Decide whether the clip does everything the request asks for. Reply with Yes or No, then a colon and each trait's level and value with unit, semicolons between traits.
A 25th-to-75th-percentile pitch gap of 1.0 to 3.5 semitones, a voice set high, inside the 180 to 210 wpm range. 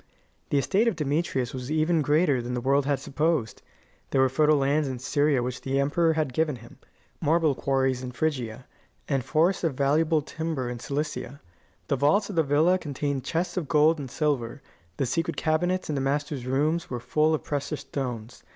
No: average, 3.0 semitones; medium, 145 Hz; average, 190 wpm